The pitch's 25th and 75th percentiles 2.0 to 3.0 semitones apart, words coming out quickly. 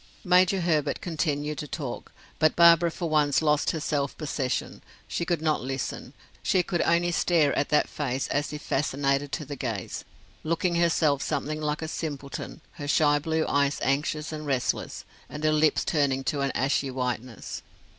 No: narrow, 2.4 semitones; average, 170 wpm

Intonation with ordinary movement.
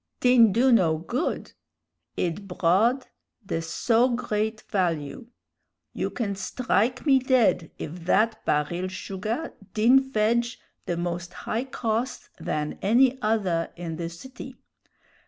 No: wide, 5.9 semitones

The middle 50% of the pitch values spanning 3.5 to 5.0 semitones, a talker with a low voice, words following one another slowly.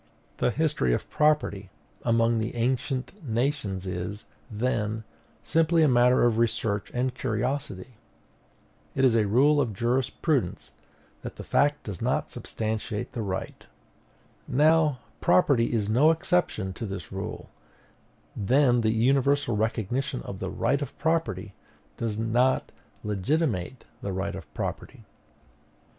Yes: average, 4.6 semitones; low, 120 Hz; slow, 125 wpm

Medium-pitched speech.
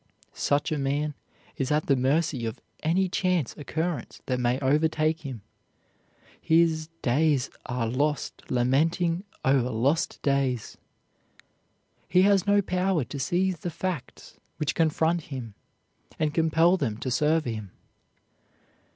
Yes: medium, 150 Hz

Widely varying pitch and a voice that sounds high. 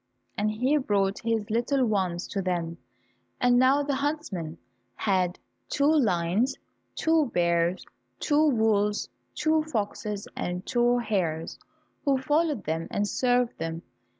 Yes: wide, 6.8 semitones; high, 220 Hz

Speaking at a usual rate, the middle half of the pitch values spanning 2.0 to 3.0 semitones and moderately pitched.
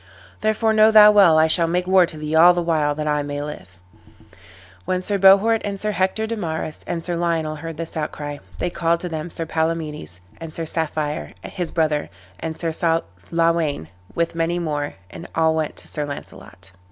Yes: average, 190 wpm; narrow, 2.5 semitones; medium, 165 Hz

